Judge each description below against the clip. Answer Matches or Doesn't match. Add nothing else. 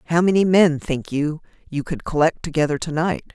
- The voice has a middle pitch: Matches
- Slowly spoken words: Doesn't match